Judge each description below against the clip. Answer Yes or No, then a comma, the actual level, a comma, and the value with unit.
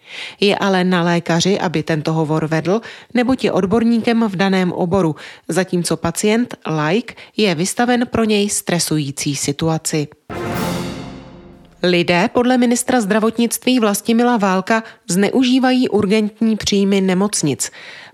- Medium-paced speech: No, slow, 110 wpm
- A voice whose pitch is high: Yes, high, 195 Hz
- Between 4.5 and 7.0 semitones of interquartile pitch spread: Yes, wide, 5.5 semitones